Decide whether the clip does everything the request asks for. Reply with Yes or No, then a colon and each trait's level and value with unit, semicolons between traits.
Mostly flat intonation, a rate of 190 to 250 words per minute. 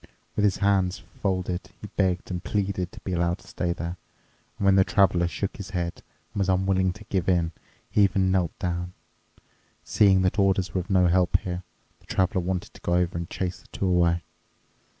Yes: narrow, 1.6 semitones; average, 200 wpm